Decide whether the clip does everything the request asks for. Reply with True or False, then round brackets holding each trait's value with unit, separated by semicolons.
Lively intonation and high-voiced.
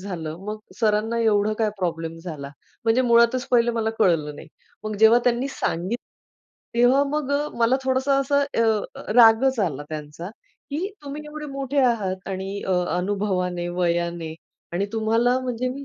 True (6.0 semitones; 220 Hz)